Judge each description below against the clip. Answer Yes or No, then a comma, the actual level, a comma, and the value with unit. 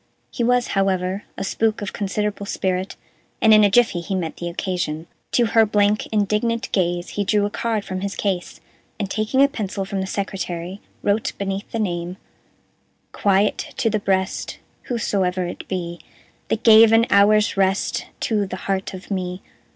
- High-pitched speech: Yes, high, 200 Hz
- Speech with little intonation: Yes, narrow, 2.3 semitones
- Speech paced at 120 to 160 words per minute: No, average, 170 wpm